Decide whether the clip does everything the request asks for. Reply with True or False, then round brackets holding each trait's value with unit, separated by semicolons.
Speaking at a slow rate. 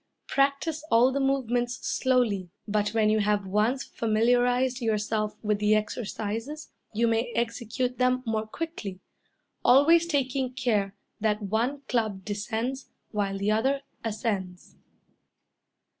True (120 wpm)